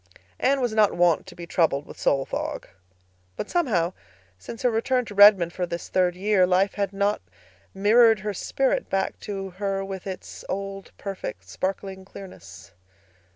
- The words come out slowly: No, average, 160 wpm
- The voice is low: No, high, 195 Hz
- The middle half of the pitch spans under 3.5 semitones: Yes, narrow, 2.6 semitones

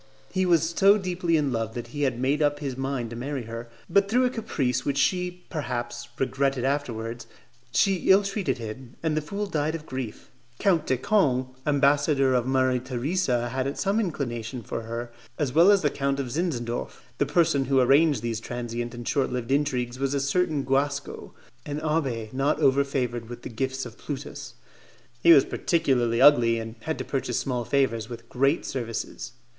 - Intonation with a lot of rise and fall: No, average, 4.0 semitones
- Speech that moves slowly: No, average, 185 wpm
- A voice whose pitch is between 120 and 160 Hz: Yes, low, 135 Hz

